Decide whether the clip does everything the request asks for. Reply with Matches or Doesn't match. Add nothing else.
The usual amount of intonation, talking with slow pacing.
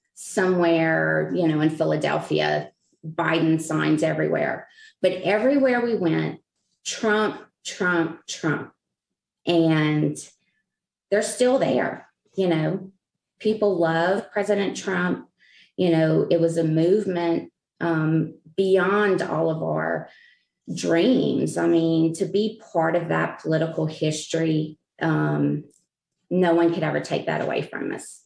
Matches